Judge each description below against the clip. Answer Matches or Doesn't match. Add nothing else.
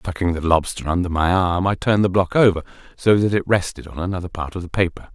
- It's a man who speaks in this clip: Matches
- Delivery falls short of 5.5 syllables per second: Doesn't match